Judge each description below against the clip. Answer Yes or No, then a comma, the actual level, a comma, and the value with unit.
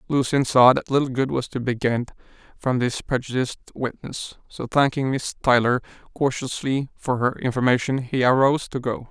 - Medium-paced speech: Yes, average, 165 wpm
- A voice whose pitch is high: No, low, 130 Hz